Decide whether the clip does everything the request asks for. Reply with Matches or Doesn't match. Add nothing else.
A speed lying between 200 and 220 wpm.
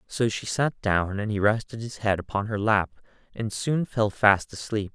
Matches